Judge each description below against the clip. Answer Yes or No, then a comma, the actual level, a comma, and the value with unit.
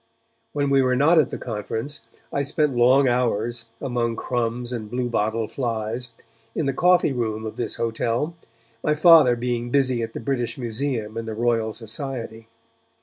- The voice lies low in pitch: Yes, low, 120 Hz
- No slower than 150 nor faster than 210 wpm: Yes, average, 160 wpm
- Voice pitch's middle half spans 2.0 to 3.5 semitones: Yes, average, 3.1 semitones